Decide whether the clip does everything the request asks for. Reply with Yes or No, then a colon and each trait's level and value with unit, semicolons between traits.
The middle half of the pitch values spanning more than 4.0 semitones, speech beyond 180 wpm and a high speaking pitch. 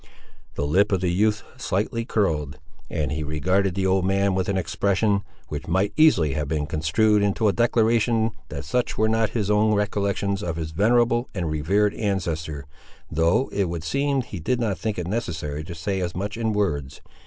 No: average, 4.8 semitones; average, 190 wpm; low, 100 Hz